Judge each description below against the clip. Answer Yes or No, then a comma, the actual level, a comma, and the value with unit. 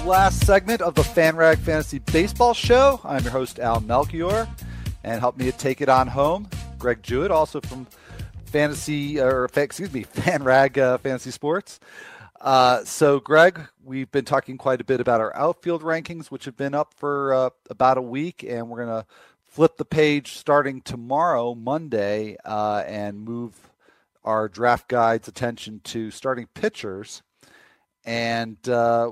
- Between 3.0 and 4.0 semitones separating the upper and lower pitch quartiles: No, average, 4.4 semitones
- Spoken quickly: No, average, 160 wpm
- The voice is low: Yes, low, 130 Hz